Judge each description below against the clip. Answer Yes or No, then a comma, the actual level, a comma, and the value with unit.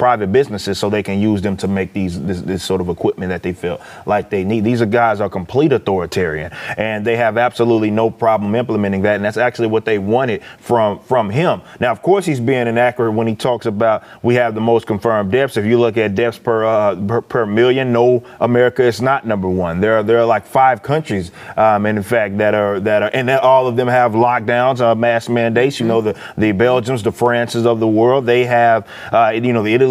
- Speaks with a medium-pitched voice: No, low, 115 Hz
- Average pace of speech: No, fast, 235 wpm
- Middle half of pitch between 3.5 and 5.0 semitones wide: No, narrow, 2.6 semitones